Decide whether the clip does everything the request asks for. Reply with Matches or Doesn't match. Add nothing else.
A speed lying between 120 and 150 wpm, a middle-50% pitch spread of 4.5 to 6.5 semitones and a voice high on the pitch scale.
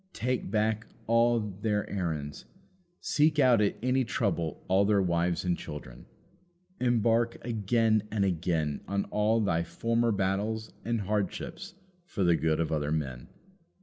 Doesn't match